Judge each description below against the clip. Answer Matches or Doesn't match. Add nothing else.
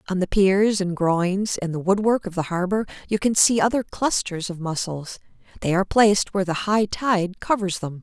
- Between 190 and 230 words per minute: Matches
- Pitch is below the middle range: Doesn't match